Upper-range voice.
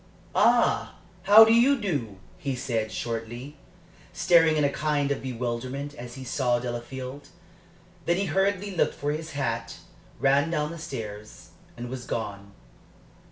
No: low, 135 Hz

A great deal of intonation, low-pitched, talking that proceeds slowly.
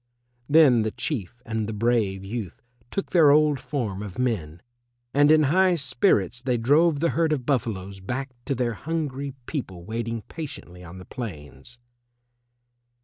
No: wide, 6.1 semitones; low, 120 Hz; average, 150 wpm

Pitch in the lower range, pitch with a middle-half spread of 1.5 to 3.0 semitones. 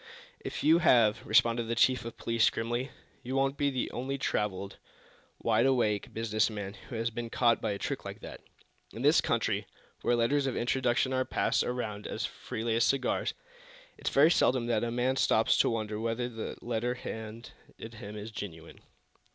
Yes: low, 115 Hz; narrow, 2.5 semitones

